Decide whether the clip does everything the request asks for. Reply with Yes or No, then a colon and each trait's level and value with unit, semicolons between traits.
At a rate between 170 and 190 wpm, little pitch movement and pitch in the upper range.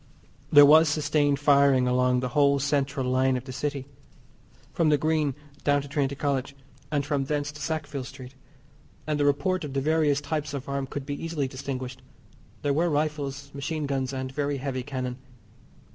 No: average, 175 wpm; narrow, 1.8 semitones; medium, 140 Hz